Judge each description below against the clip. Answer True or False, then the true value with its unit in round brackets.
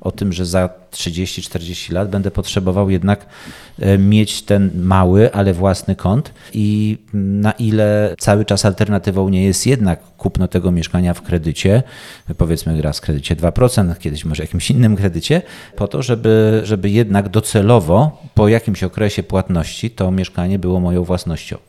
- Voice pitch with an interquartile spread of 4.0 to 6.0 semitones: False (2.9 semitones)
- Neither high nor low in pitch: False (100 Hz)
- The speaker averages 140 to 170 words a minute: True (150 wpm)